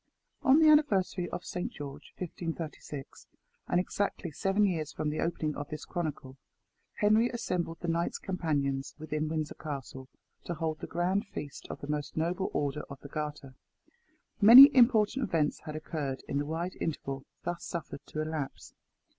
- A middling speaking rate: Yes, average, 160 wpm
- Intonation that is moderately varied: Yes, average, 3.8 semitones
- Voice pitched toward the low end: No, medium, 160 Hz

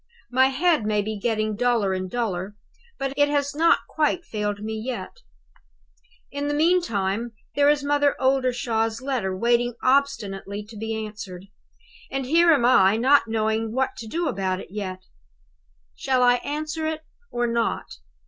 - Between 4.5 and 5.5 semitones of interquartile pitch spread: Yes, average, 5.0 semitones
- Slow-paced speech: No, average, 155 wpm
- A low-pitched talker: No, high, 240 Hz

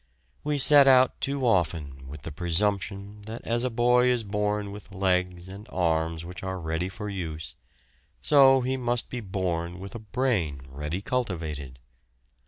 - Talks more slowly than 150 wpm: No, average, 160 wpm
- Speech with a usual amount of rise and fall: No, wide, 6.0 semitones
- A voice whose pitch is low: Yes, very low, 95 Hz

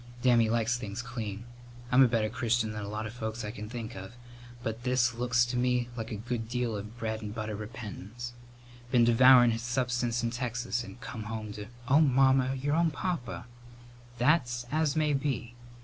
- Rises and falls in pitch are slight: Yes, narrow, 2.2 semitones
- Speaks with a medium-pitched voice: No, low, 120 Hz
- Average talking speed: Yes, average, 195 wpm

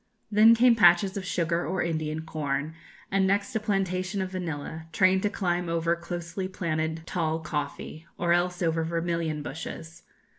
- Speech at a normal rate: Yes, average, 155 wpm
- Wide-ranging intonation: No, average, 2.8 semitones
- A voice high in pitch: No, medium, 170 Hz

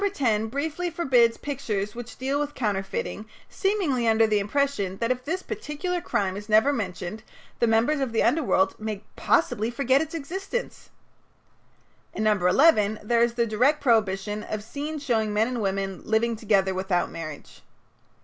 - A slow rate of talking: No, average, 160 wpm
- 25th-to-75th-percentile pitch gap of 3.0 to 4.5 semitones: No, average, 5.2 semitones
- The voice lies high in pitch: Yes, high, 230 Hz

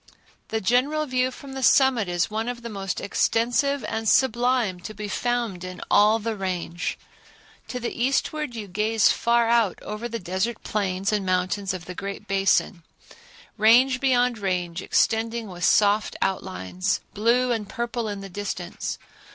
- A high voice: Yes, high, 220 Hz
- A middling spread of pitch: Yes, average, 3.8 semitones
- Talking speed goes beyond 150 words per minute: Yes, average, 160 wpm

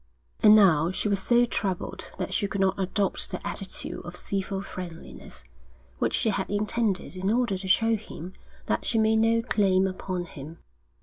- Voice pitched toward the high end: Yes, high, 195 Hz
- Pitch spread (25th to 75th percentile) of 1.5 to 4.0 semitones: Yes, average, 2.8 semitones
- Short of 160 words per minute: No, average, 175 wpm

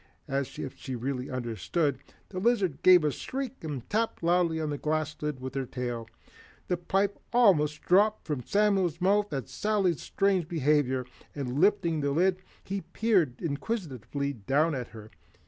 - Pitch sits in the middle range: Yes, medium, 155 Hz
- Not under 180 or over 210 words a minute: No, average, 160 wpm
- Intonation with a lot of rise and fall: Yes, wide, 6.0 semitones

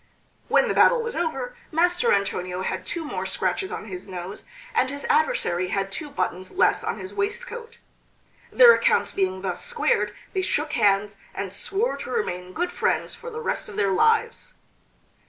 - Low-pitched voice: No, very high, 295 Hz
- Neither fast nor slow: Yes, average, 175 wpm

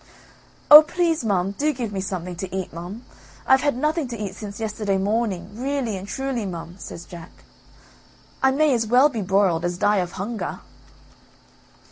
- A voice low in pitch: No, high, 210 Hz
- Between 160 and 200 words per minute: Yes, average, 170 wpm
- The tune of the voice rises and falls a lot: Yes, wide, 5.7 semitones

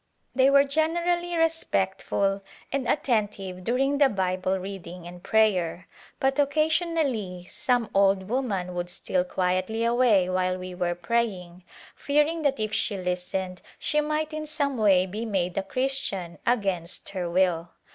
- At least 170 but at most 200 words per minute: No, average, 145 wpm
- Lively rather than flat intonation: Yes, wide, 6.8 semitones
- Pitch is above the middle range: Yes, high, 200 Hz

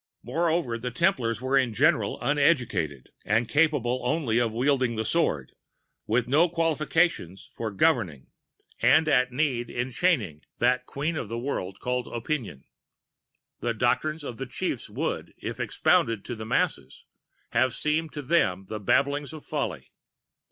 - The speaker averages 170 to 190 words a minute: No, average, 145 wpm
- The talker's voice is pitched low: Yes, low, 125 Hz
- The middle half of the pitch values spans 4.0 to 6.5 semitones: Yes, average, 5.1 semitones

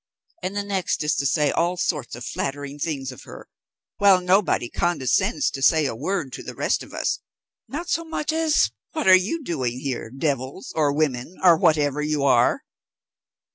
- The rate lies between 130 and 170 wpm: No, average, 180 wpm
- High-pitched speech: No, medium, 155 Hz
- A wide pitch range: Yes, wide, 5.7 semitones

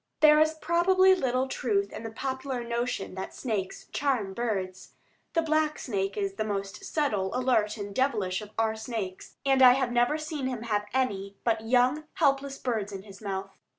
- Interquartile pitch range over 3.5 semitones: Yes, average, 5.2 semitones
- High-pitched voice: Yes, high, 240 Hz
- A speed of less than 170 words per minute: No, average, 180 wpm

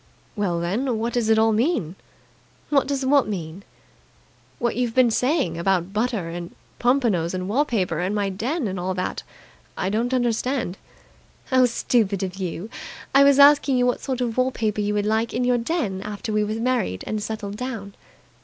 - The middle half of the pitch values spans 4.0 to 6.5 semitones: Yes, average, 4.4 semitones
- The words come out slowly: No, average, 185 wpm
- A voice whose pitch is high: Yes, high, 220 Hz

